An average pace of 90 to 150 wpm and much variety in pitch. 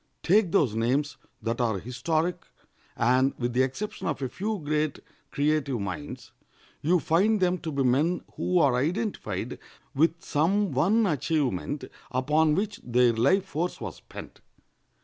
Yes: average, 145 wpm; wide, 5.9 semitones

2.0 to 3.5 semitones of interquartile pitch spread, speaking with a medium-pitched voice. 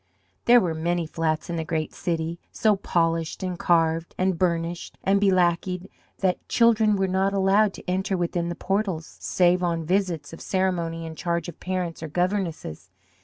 Yes: narrow, 2.4 semitones; medium, 175 Hz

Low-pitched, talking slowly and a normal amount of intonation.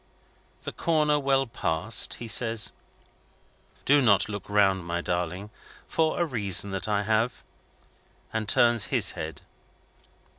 Yes: low, 110 Hz; slow, 125 wpm; average, 4.4 semitones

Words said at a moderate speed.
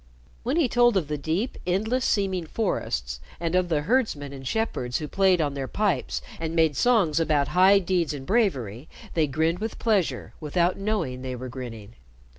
Yes: average, 180 wpm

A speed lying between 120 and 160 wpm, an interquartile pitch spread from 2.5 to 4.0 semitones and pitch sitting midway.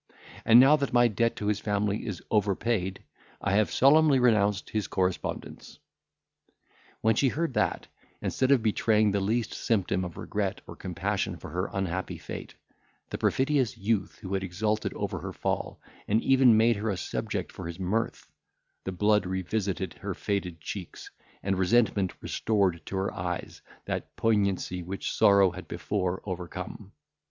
No: average, 155 wpm; average, 3.3 semitones; low, 100 Hz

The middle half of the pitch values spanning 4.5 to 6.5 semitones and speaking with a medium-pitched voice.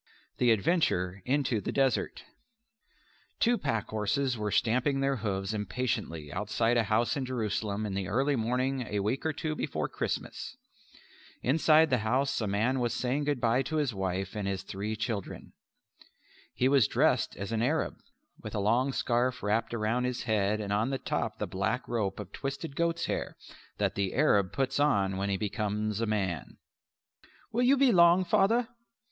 No: average, 4.8 semitones; low, 115 Hz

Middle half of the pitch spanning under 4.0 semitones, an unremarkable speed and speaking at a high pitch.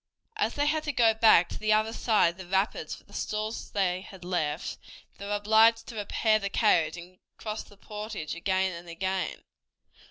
Yes: average, 3.2 semitones; average, 195 wpm; high, 205 Hz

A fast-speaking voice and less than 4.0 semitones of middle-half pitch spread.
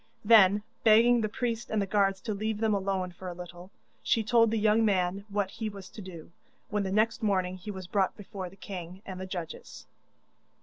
Yes: fast, 210 wpm; narrow, 2.6 semitones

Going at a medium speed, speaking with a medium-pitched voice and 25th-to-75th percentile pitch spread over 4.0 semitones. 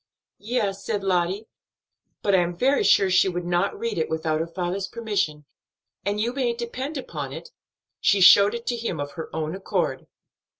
No: average, 180 wpm; high, 195 Hz; average, 5.0 semitones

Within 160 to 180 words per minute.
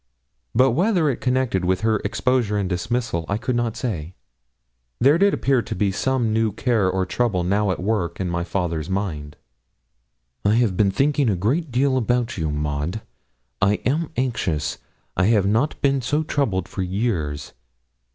Yes: average, 165 wpm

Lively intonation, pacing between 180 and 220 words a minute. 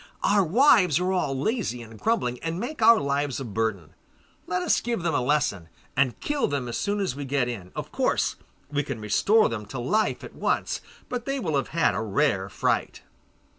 Yes: wide, 8.9 semitones; fast, 205 wpm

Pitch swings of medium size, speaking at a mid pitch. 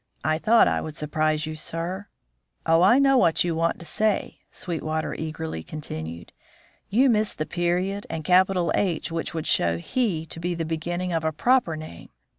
Yes: average, 3.1 semitones; medium, 165 Hz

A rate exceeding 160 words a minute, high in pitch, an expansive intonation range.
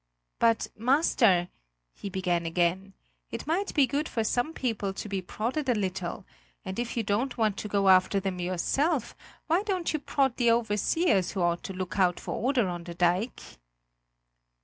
Yes: average, 175 wpm; high, 210 Hz; wide, 5.7 semitones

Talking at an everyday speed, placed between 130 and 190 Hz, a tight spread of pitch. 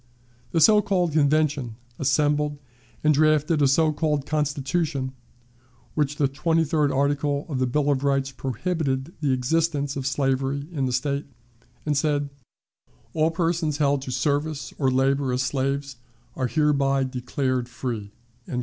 Yes: average, 145 wpm; medium, 140 Hz; narrow, 2.3 semitones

